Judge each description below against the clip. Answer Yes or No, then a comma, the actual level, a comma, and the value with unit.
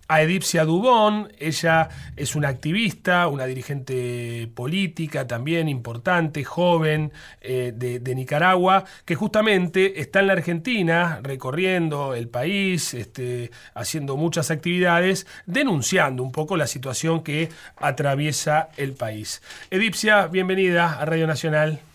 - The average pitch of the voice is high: No, medium, 160 Hz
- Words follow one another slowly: Yes, slow, 120 wpm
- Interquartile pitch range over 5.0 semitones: No, average, 4.7 semitones